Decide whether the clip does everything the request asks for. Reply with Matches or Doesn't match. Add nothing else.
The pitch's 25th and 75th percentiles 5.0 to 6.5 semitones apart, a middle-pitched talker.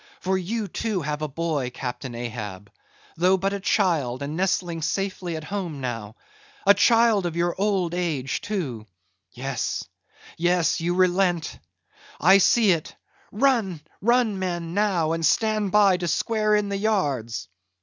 Matches